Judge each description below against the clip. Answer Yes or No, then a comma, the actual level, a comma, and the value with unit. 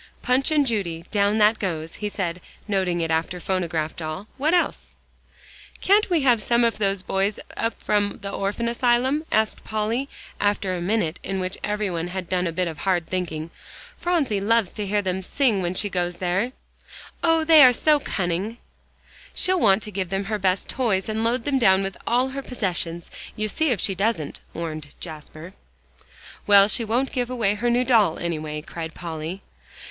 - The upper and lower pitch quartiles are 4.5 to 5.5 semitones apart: Yes, average, 4.9 semitones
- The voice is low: No, high, 200 Hz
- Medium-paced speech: Yes, average, 185 wpm